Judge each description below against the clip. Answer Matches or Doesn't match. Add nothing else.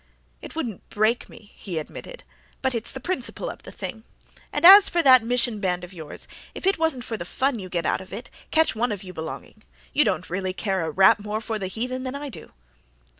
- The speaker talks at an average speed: Doesn't match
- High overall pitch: Matches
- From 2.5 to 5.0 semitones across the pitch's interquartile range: Doesn't match